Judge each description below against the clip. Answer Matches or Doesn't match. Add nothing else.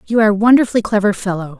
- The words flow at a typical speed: Doesn't match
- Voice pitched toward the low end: Doesn't match